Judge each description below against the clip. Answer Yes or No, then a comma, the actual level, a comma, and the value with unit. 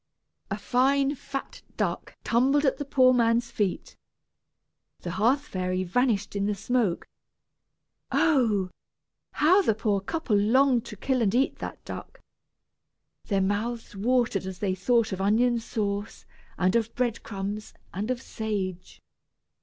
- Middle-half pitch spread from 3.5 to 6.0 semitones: Yes, average, 4.2 semitones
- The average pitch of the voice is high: Yes, high, 225 Hz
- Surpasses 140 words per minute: No, slow, 135 wpm